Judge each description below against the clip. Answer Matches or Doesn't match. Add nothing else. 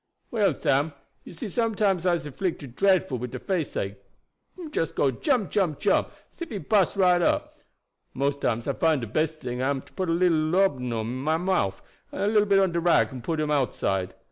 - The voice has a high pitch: Doesn't match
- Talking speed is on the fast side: Matches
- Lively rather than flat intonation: Matches